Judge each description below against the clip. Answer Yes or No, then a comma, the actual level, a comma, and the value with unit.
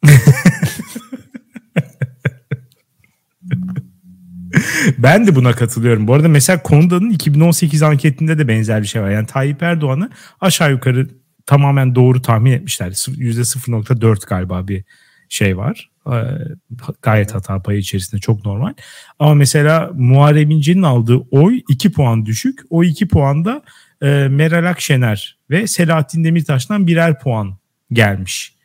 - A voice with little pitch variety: No, wide, 5.6 semitones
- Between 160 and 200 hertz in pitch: No, medium, 140 Hz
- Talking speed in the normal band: Yes, average, 115 wpm